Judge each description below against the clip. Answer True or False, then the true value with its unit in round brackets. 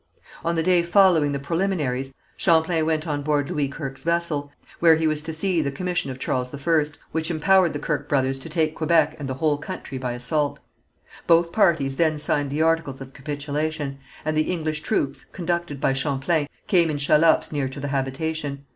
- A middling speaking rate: True (190 wpm)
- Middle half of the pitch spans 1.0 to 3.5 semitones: True (2.9 semitones)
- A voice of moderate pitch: True (155 Hz)